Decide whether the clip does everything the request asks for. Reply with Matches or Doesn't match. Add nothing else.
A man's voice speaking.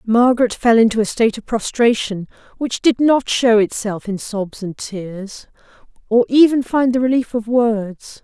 Doesn't match